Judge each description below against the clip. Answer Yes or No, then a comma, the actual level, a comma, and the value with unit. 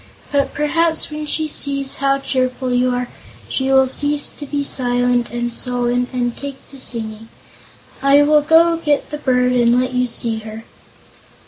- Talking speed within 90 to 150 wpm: No, average, 165 wpm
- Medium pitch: No, very high, 260 Hz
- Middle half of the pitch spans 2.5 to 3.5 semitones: Yes, average, 2.8 semitones